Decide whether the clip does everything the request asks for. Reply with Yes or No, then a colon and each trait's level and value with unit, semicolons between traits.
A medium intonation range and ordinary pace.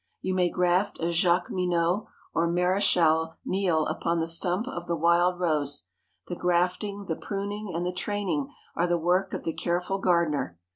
No: narrow, 1.9 semitones; average, 160 wpm